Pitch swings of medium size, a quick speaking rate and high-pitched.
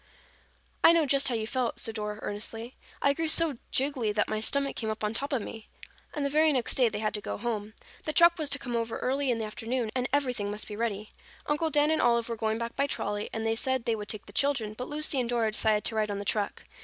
Yes: average, 4.4 semitones; fast, 265 wpm; high, 235 Hz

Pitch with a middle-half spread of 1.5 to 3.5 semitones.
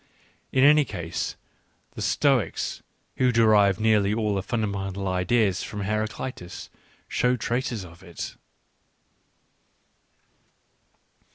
Yes: average, 3.2 semitones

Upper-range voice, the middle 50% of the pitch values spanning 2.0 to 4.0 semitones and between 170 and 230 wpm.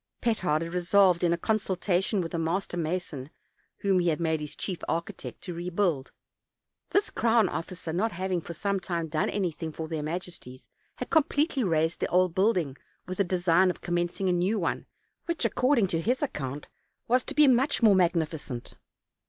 No: medium, 180 Hz; average, 3.4 semitones; average, 180 wpm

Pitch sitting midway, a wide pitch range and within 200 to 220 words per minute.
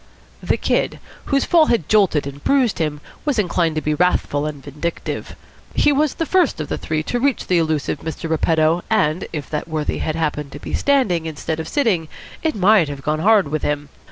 Yes: medium, 160 Hz; wide, 6.2 semitones; fast, 205 wpm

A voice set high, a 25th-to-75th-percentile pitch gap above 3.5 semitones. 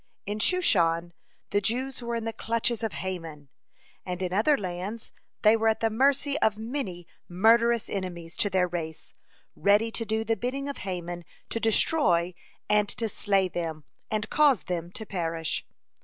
Yes: high, 210 Hz; average, 4.5 semitones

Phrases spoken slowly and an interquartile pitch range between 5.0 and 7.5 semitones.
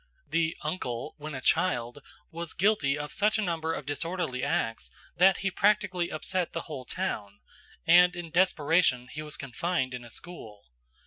No: average, 165 wpm; wide, 5.4 semitones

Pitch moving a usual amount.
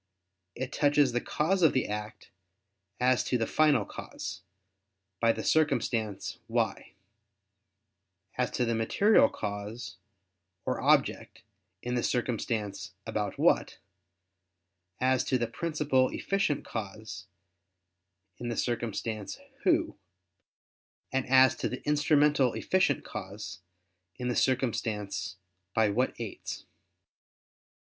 Yes: average, 4.2 semitones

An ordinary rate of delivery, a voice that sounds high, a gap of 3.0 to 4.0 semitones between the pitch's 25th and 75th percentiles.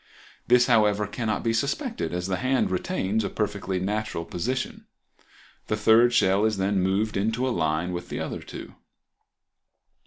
No: average, 155 wpm; low, 105 Hz; average, 3.5 semitones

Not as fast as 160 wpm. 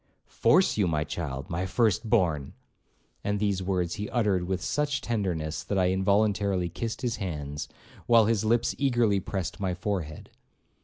Yes: average, 150 wpm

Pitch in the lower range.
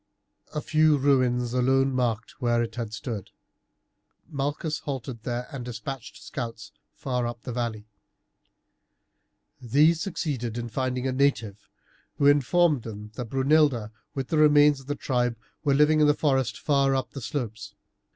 Yes: low, 130 Hz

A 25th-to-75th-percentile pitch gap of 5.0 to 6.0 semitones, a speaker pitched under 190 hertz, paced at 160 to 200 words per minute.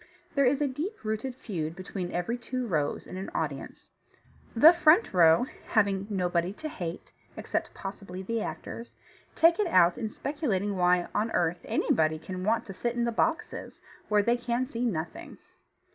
No: wide, 5.6 semitones; high, 210 Hz; average, 170 wpm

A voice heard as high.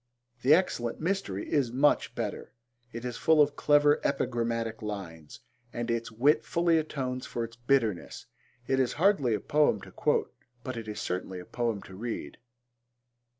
No: low, 120 Hz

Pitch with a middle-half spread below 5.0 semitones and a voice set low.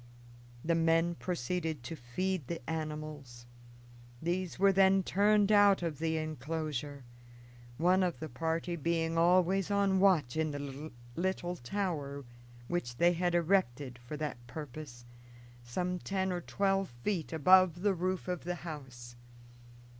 No: average, 4.0 semitones; medium, 165 Hz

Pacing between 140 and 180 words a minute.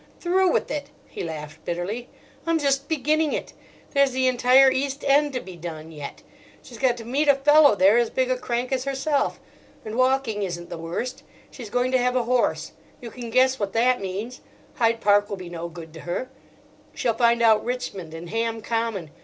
No: average, 195 wpm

